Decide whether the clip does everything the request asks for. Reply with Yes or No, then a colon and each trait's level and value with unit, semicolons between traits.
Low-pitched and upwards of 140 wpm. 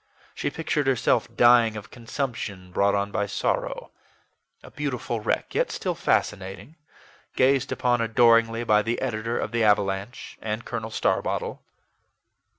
No: low, 115 Hz; slow, 135 wpm